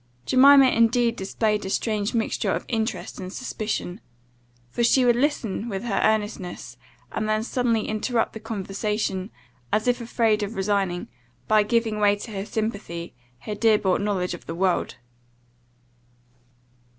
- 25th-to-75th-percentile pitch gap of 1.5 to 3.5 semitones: Yes, average, 2.7 semitones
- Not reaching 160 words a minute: Yes, average, 150 wpm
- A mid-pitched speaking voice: No, high, 215 Hz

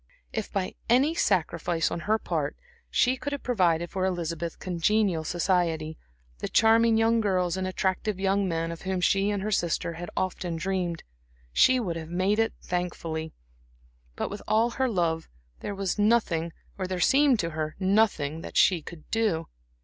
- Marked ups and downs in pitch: No, average, 4.2 semitones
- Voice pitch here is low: No, medium, 185 Hz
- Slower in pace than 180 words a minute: Yes, average, 170 wpm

